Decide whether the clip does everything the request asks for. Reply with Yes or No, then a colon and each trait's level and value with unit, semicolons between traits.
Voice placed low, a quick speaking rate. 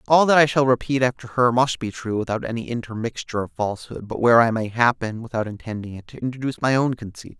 Yes: low, 120 Hz; fast, 225 wpm